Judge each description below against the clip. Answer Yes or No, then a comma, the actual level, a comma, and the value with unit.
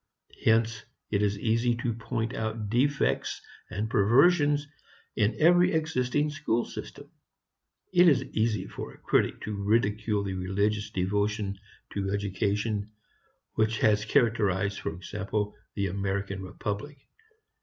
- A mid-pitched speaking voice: No, low, 110 Hz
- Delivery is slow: Yes, slow, 125 wpm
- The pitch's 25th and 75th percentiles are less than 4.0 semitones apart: Yes, average, 2.8 semitones